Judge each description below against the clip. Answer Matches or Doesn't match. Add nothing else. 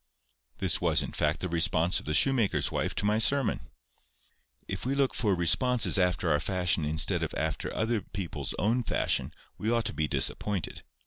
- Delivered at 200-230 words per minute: Doesn't match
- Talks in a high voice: Doesn't match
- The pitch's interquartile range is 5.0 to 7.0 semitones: Matches